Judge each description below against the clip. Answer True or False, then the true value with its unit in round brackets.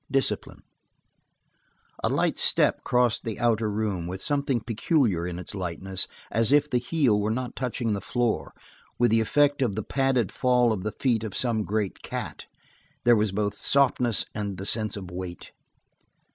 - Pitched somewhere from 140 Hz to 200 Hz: False (110 Hz)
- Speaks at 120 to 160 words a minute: False (170 wpm)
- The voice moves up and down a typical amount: True (3.6 semitones)